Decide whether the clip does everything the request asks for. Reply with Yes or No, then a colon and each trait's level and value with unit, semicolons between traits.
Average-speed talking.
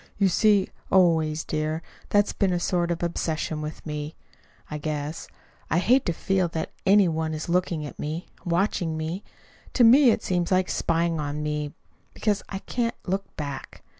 Yes: average, 175 wpm